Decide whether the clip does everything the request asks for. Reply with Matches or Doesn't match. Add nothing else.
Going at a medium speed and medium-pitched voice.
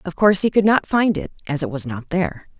Doesn't match